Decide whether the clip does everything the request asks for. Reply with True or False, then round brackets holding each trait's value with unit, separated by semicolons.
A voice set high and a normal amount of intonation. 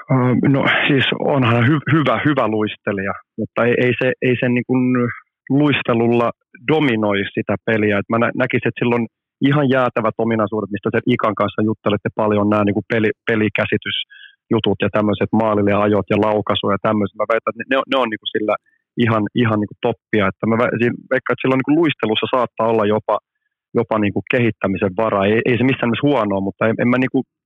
False (115 Hz; 3.2 semitones)